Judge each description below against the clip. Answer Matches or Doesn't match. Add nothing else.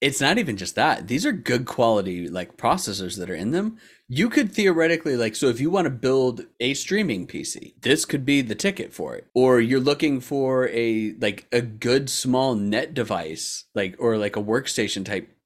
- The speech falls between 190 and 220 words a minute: Matches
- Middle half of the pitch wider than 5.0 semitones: Matches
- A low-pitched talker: Matches